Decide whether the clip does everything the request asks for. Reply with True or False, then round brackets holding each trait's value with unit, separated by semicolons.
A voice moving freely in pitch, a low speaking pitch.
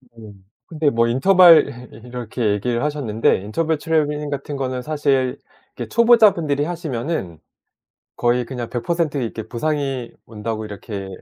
False (4.9 semitones; 130 Hz)